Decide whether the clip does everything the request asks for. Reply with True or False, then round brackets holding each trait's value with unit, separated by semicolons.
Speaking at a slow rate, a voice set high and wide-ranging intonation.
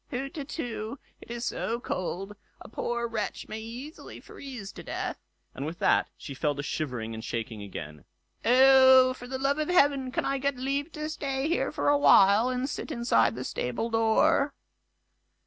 False (170 wpm; 245 Hz; 6.1 semitones)